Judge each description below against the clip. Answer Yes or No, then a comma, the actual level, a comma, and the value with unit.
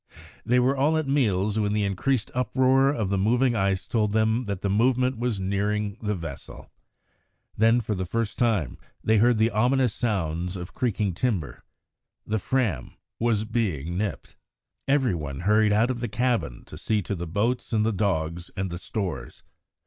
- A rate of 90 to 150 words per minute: No, average, 175 wpm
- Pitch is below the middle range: Yes, low, 105 Hz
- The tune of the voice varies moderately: Yes, average, 4.1 semitones